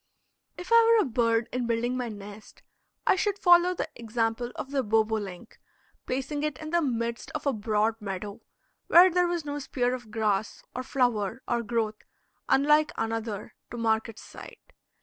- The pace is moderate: Yes, average, 170 wpm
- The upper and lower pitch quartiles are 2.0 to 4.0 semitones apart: No, average, 4.7 semitones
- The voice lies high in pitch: Yes, high, 240 Hz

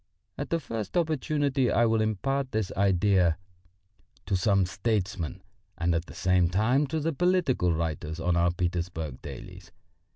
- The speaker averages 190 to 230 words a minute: No, average, 150 wpm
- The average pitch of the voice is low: Yes, low, 100 Hz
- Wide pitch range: Yes, wide, 7.1 semitones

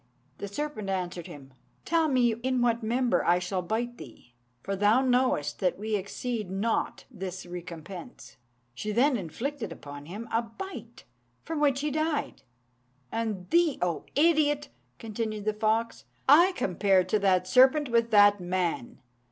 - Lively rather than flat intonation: Yes, wide, 5.7 semitones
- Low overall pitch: No, high, 220 Hz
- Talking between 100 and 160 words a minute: Yes, average, 150 wpm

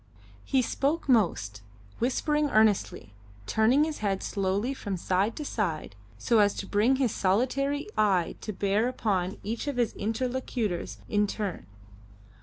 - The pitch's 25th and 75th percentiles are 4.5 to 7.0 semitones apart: Yes, average, 4.8 semitones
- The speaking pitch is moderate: No, high, 215 Hz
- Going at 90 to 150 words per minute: Yes, average, 140 wpm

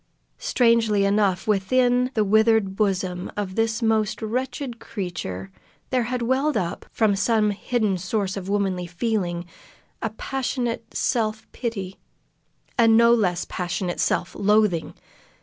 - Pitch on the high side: Yes, high, 215 Hz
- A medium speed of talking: No, slow, 125 wpm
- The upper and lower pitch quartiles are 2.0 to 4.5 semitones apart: Yes, average, 3.4 semitones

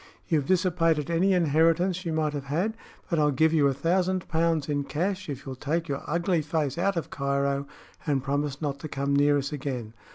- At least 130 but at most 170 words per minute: No, average, 200 wpm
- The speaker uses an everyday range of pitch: Yes, average, 3.3 semitones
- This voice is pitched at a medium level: Yes, medium, 155 Hz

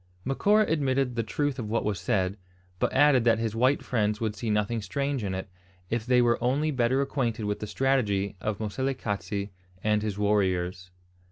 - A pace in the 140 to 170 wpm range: No, average, 180 wpm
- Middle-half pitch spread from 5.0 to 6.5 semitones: No, average, 4.2 semitones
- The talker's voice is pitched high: No, low, 115 Hz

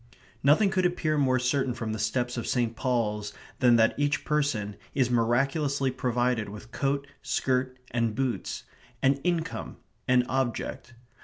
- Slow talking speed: No, average, 145 wpm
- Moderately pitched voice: No, low, 125 Hz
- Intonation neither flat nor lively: Yes, average, 3.0 semitones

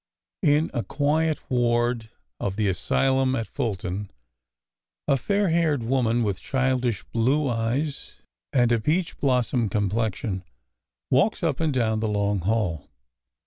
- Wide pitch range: No, average, 4.3 semitones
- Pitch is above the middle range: No, low, 120 Hz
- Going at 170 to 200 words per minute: No, slow, 135 wpm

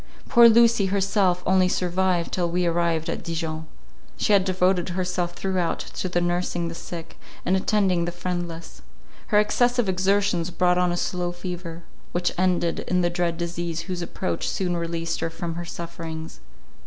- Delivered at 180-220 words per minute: No, average, 165 wpm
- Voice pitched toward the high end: No, medium, 175 Hz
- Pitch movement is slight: Yes, narrow, 1.6 semitones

